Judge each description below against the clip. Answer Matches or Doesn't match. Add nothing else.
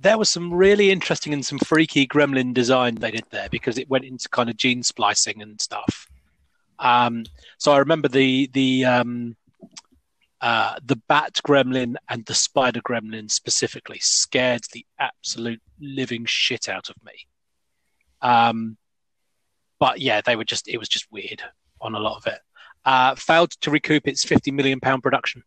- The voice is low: Matches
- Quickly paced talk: Doesn't match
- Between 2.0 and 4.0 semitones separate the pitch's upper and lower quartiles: Matches